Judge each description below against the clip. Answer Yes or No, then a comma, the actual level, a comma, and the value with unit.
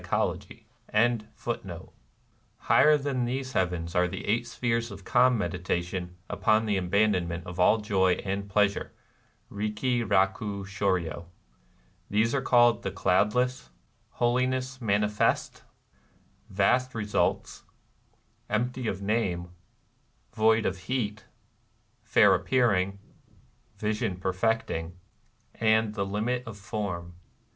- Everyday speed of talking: No, slow, 105 wpm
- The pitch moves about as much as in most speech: Yes, average, 3.9 semitones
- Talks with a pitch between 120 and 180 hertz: No, low, 105 Hz